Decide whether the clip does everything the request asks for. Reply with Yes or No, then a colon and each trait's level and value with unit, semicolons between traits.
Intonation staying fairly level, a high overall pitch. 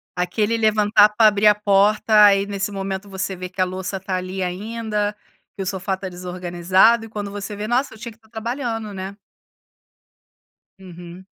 Yes: narrow, 2.3 semitones; high, 200 Hz